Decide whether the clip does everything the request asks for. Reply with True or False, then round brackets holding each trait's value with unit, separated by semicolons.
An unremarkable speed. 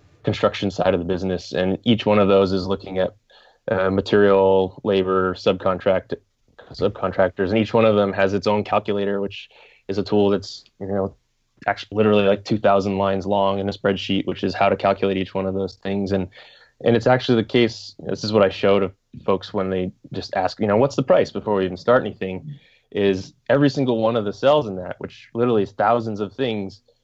False (215 wpm)